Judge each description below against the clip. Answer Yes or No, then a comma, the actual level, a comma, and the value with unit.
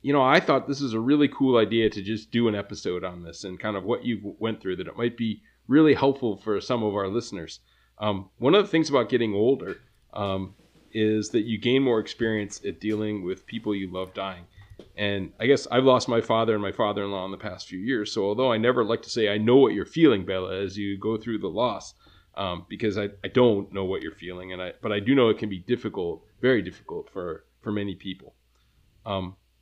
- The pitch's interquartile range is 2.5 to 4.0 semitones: Yes, average, 3.6 semitones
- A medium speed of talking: No, fast, 235 wpm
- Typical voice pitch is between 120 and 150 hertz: No, low, 105 Hz